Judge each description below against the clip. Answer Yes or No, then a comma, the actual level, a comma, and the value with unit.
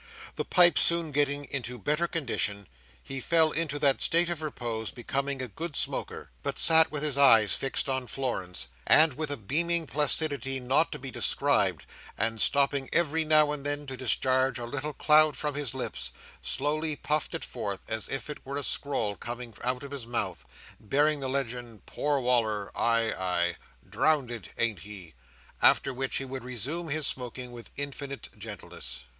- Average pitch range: Yes, average, 3.9 semitones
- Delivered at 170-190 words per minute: Yes, average, 175 wpm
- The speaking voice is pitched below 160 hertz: Yes, low, 135 Hz